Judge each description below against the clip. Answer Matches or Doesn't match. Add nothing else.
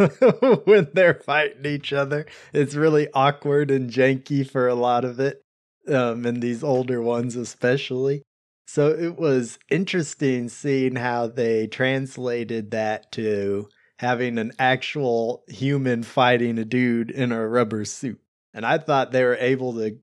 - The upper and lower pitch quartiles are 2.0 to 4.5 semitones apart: Matches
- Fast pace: Doesn't match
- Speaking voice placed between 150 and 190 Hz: Doesn't match